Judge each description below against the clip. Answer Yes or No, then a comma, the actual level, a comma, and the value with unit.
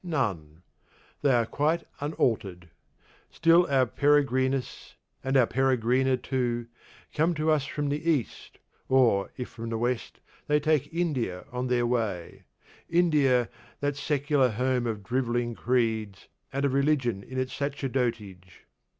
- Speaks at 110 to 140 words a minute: Yes, slow, 135 wpm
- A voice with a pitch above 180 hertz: No, low, 130 Hz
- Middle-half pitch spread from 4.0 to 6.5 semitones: No, average, 3.6 semitones